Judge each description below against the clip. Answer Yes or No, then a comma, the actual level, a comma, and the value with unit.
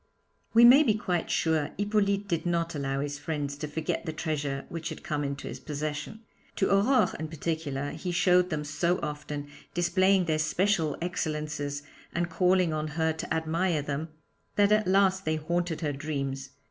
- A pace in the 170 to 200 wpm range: Yes, average, 175 wpm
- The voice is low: No, medium, 160 Hz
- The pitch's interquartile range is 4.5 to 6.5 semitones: No, average, 3.6 semitones